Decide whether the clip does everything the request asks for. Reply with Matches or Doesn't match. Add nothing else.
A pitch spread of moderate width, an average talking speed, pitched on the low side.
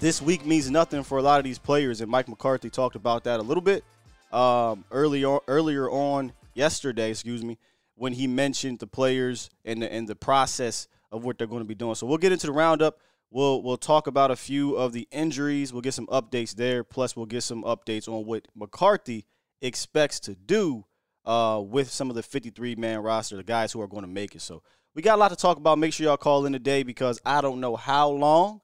Doesn't match